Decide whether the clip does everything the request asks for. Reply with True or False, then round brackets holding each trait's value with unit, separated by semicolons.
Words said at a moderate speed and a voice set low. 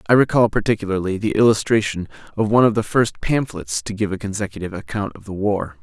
True (195 wpm; 105 Hz)